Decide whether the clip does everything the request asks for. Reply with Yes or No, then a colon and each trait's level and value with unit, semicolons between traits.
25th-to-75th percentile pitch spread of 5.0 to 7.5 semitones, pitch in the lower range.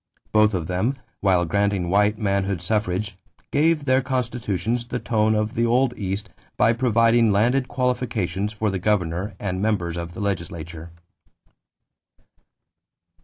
No: average, 4.0 semitones; low, 105 Hz